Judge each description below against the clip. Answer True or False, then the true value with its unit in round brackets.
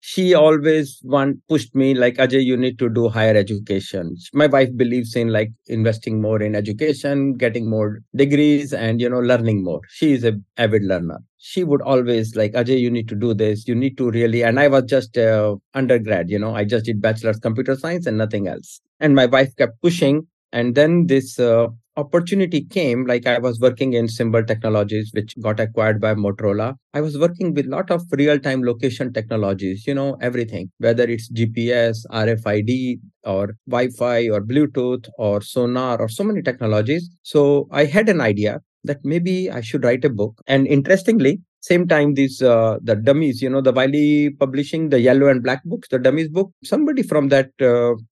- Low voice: True (125 Hz)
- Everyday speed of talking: True (195 wpm)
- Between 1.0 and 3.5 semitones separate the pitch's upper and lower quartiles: False (4.2 semitones)